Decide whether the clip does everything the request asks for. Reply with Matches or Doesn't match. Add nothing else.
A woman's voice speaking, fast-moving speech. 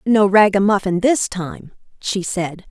Doesn't match